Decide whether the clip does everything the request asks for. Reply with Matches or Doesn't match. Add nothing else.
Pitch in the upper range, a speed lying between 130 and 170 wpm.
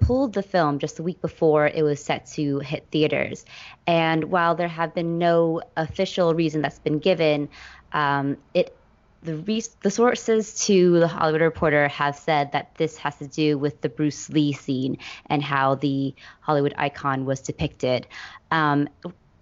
Doesn't match